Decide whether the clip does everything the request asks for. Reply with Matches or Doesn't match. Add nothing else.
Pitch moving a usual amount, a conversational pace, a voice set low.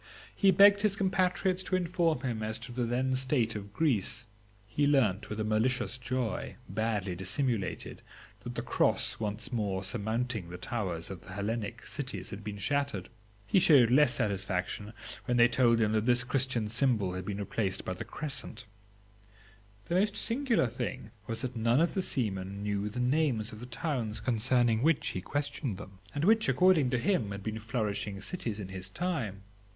Matches